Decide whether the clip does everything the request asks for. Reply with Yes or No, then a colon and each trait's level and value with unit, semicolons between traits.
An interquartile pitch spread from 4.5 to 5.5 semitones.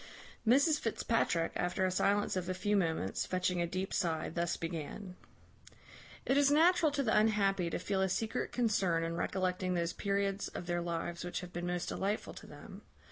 No: average, 3.2 semitones